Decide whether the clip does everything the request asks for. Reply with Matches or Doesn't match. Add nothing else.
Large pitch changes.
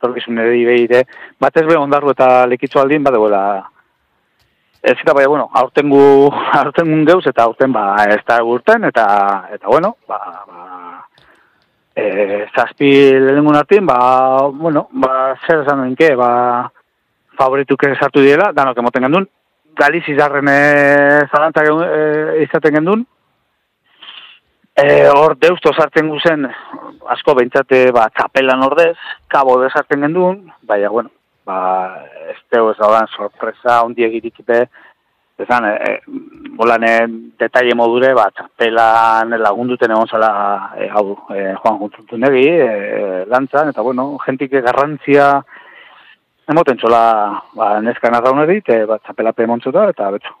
Doesn't match